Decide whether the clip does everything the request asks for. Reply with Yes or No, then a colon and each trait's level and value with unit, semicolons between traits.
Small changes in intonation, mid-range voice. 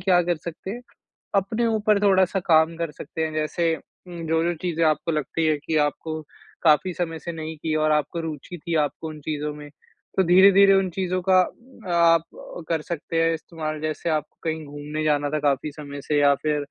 Yes: narrow, 2.3 semitones; medium, 160 Hz